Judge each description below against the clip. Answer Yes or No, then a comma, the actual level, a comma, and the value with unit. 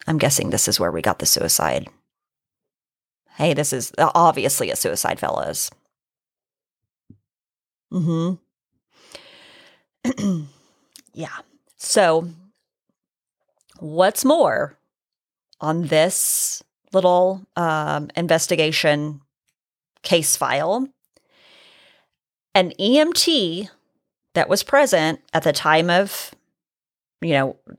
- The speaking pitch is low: No, medium, 180 Hz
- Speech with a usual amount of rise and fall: No, wide, 7.9 semitones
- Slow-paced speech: Yes, slow, 85 wpm